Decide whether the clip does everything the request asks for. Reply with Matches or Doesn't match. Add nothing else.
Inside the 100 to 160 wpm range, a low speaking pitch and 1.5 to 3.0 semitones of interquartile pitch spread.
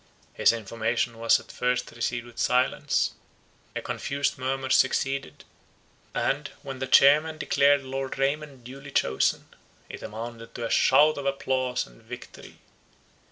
Matches